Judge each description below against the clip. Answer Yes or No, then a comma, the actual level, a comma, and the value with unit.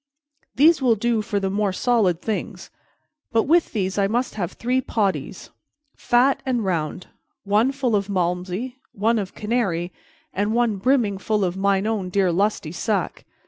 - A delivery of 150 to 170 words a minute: Yes, average, 160 wpm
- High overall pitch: Yes, high, 205 Hz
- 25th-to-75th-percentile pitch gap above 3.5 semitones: Yes, average, 3.9 semitones